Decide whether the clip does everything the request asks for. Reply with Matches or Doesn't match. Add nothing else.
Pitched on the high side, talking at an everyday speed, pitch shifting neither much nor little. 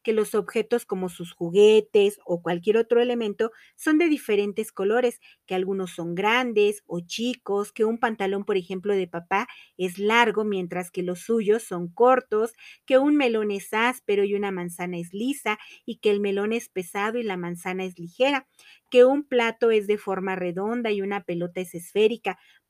Matches